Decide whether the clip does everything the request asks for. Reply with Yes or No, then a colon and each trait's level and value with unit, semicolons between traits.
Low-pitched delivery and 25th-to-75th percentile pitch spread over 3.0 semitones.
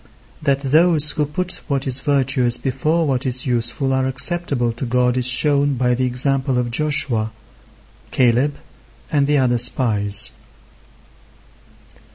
No: low, 130 Hz; average, 2.7 semitones